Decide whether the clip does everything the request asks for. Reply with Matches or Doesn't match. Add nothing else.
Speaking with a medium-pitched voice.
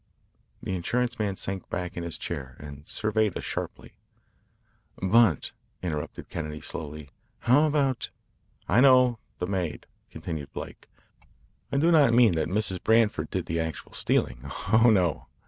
Doesn't match